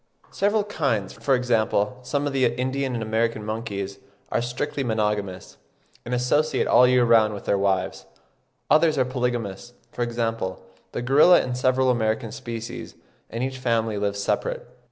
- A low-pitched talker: Yes, low, 120 Hz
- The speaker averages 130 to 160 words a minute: Yes, average, 155 wpm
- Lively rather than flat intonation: No, average, 3.2 semitones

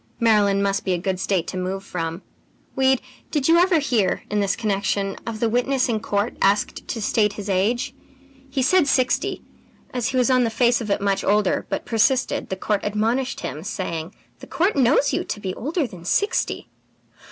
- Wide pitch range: No, average, 4.6 semitones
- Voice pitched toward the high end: Yes, high, 215 Hz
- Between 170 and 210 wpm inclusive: Yes, average, 195 wpm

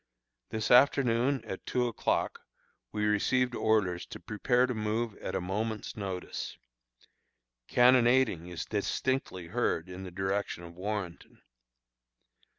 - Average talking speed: No, slow, 120 wpm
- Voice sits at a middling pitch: No, low, 105 Hz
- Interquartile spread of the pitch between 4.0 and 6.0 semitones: Yes, average, 4.6 semitones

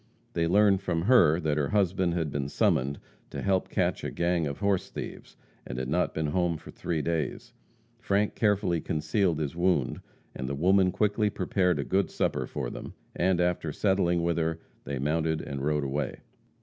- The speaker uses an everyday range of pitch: Yes, average, 3.9 semitones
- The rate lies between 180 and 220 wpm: Yes, average, 185 wpm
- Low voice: Yes, very low, 85 Hz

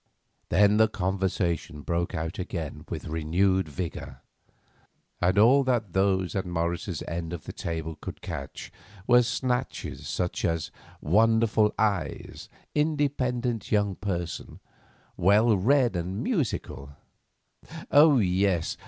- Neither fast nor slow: No, slow, 115 wpm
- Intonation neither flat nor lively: Yes, average, 5.0 semitones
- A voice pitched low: Yes, very low, 95 Hz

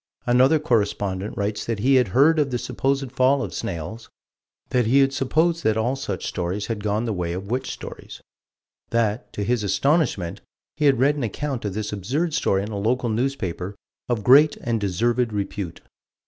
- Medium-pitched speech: No, low, 115 Hz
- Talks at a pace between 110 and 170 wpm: No, average, 185 wpm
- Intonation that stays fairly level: No, average, 4.8 semitones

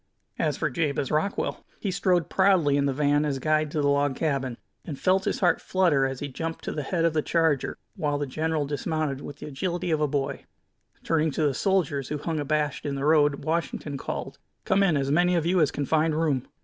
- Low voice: No, medium, 150 Hz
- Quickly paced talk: Yes, fast, 225 wpm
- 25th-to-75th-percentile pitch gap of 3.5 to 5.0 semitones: No, narrow, 2.6 semitones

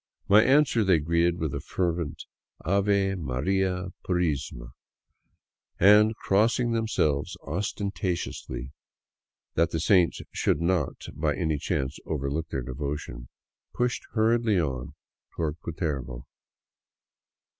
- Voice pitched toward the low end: Yes, very low, 85 Hz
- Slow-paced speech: Yes, slow, 115 wpm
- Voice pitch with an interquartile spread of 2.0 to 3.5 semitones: No, average, 5.3 semitones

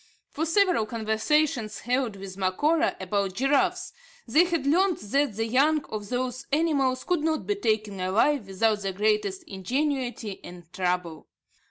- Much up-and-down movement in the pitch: Yes, wide, 7.0 semitones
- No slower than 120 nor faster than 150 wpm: Yes, average, 145 wpm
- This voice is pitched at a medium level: No, high, 235 Hz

